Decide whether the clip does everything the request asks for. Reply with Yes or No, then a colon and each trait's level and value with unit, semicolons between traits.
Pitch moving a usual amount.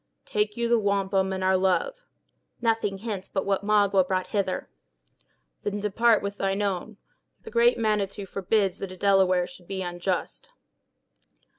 No: narrow, 1.9 semitones